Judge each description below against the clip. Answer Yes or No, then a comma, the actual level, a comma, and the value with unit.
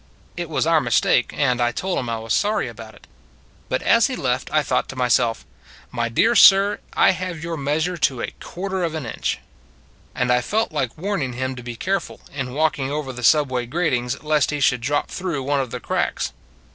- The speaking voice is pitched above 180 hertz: No, medium, 140 Hz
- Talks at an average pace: No, fast, 220 wpm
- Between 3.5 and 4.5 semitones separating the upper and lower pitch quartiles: No, wide, 5.4 semitones